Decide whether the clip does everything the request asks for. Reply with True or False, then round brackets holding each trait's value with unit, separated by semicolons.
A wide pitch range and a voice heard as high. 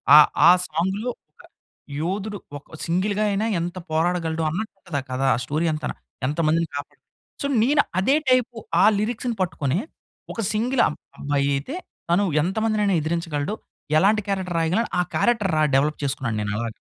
False (5.7 semitones; 175 Hz)